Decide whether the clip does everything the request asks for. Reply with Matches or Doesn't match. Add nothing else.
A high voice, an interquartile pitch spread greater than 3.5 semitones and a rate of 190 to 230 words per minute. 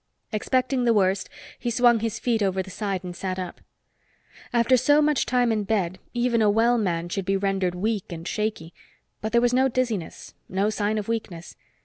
Matches